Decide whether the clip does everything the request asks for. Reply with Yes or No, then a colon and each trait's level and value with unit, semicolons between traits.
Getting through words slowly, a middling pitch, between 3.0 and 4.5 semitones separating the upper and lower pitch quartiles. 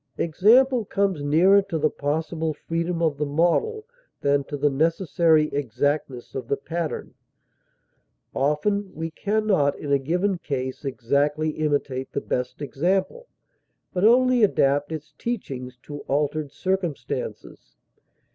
No: slow, 130 wpm; medium, 155 Hz; average, 4.9 semitones